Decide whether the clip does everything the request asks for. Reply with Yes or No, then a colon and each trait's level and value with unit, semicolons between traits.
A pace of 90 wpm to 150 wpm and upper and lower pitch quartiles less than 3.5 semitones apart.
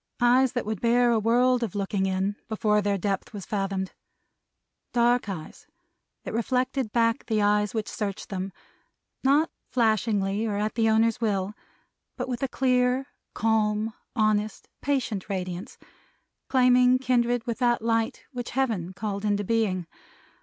Yes: average, 145 wpm; average, 3.1 semitones